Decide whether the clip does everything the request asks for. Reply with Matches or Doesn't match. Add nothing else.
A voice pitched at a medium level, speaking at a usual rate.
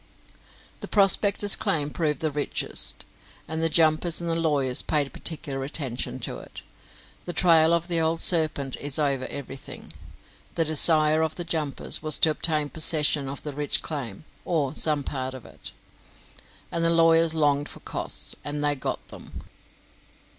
Matches